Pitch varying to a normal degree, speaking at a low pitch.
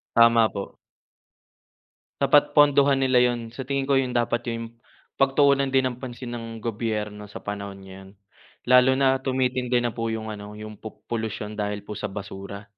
Yes: average, 3.7 semitones; low, 115 Hz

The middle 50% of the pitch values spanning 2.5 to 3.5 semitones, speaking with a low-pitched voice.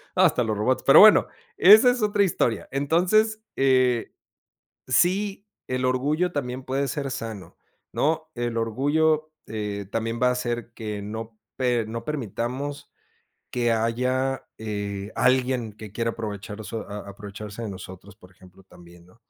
No: average, 4.5 semitones; low, 120 Hz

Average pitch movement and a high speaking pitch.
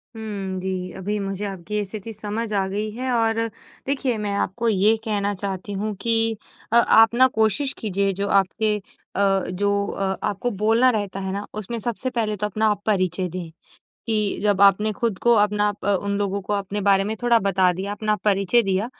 No: narrow, 2.2 semitones; high, 205 Hz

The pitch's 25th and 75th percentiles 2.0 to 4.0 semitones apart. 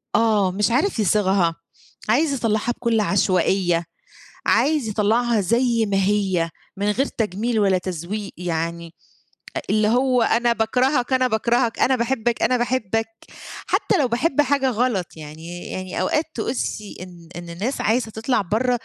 No: average, 4.6 semitones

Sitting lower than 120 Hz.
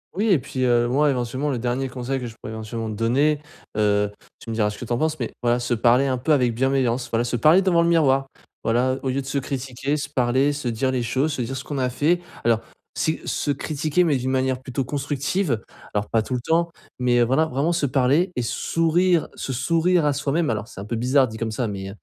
No: low, 130 Hz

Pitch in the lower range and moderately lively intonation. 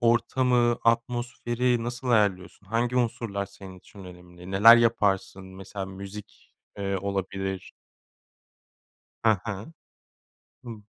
Yes: low, 105 Hz; average, 3.5 semitones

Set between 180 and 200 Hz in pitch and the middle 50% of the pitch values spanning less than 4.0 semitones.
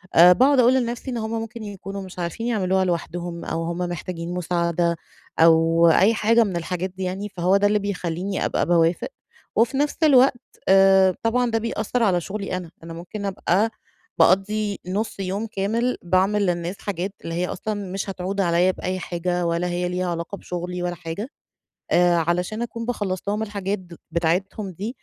Yes: high, 190 Hz; average, 3.3 semitones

